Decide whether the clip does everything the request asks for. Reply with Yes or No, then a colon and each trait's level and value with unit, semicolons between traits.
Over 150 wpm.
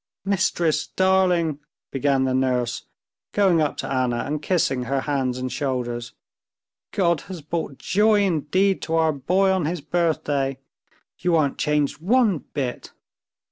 No: average, 140 wpm